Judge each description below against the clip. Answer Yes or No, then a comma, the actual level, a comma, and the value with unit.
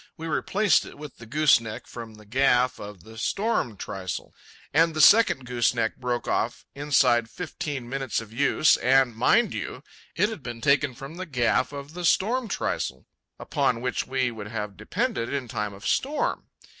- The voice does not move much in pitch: No, average, 5.2 semitones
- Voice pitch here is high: No, low, 130 Hz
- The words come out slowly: No, average, 175 wpm